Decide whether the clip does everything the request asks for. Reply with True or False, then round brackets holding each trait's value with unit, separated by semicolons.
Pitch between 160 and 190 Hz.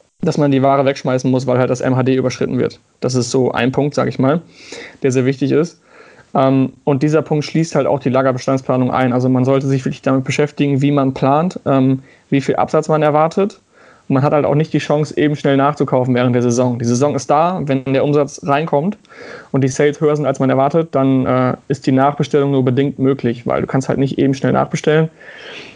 False (140 Hz)